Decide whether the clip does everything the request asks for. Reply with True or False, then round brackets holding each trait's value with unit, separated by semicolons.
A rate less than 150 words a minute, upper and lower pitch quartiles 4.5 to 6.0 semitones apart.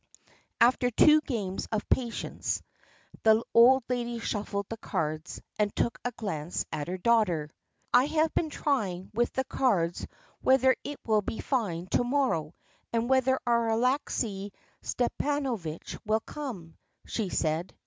True (140 wpm; 5.2 semitones)